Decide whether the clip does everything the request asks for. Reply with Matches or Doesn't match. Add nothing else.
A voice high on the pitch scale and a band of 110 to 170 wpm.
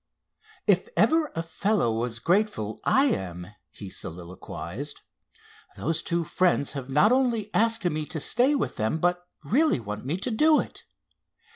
Doesn't match